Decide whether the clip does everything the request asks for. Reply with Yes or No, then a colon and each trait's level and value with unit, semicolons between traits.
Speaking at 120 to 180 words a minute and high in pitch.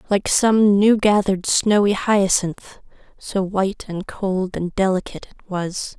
Yes: average, 140 wpm; high, 195 Hz